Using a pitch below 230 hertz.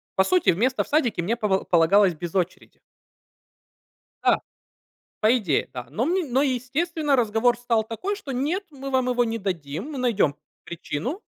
No: high, 235 Hz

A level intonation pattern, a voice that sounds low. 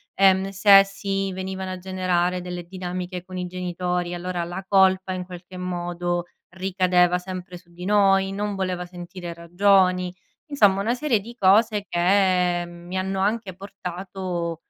No: narrow, 1.5 semitones; medium, 185 Hz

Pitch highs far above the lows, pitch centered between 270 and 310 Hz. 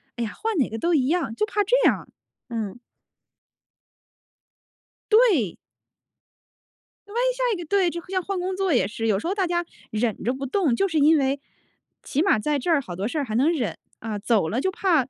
Yes: wide, 8.2 semitones; very high, 300 Hz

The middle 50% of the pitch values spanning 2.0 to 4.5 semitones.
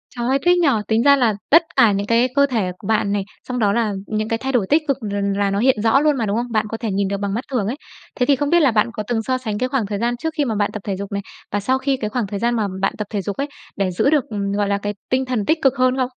Yes: average, 4.1 semitones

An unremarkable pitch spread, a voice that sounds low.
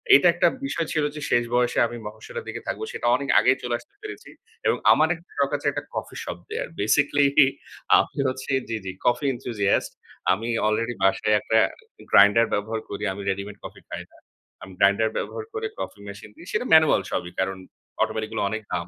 No: wide, 5.7 semitones; low, 115 Hz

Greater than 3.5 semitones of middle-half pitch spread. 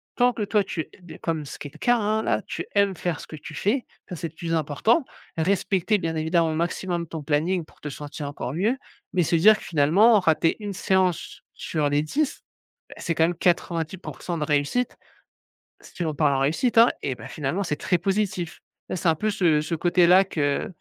Yes: average, 4.1 semitones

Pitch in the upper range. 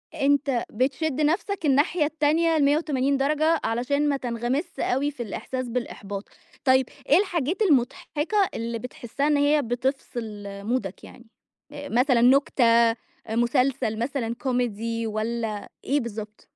Yes: very high, 260 Hz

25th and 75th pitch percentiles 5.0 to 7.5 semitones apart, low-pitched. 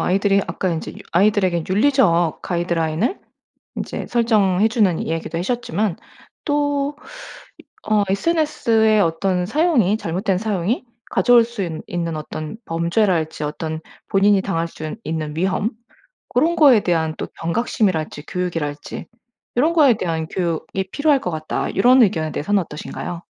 No: wide, 5.4 semitones; high, 190 Hz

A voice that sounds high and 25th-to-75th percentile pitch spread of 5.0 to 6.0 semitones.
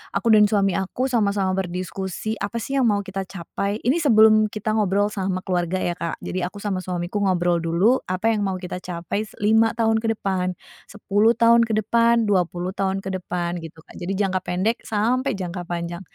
No: high, 195 Hz; average, 3.2 semitones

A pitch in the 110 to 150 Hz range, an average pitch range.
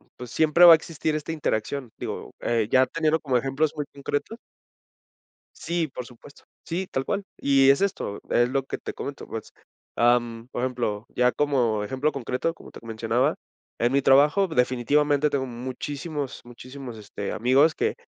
Yes: low, 135 Hz; average, 3.7 semitones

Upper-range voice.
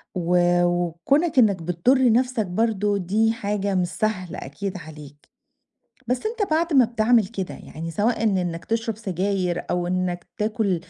Yes: high, 200 Hz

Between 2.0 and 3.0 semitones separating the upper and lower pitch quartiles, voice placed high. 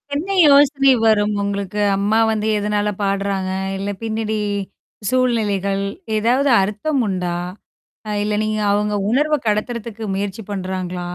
Yes: average, 2.7 semitones; high, 210 Hz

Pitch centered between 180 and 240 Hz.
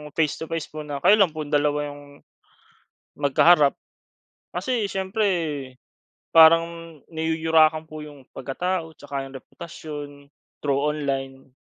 No: medium, 155 Hz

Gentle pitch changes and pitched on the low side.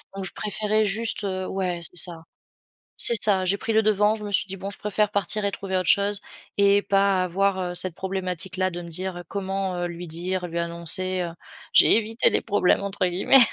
No: narrow, 2.1 semitones; high, 190 Hz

